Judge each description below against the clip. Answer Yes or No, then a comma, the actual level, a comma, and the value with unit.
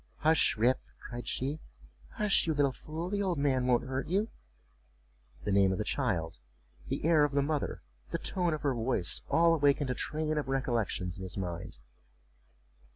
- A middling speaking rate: Yes, average, 175 wpm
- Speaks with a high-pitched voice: No, medium, 140 Hz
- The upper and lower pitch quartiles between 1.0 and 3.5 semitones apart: No, average, 5.0 semitones